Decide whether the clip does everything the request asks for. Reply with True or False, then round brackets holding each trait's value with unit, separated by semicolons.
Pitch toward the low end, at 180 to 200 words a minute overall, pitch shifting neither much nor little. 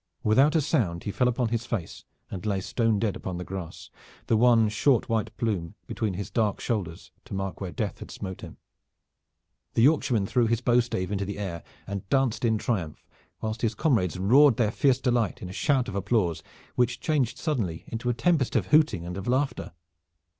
True (110 Hz; 195 wpm; 4.2 semitones)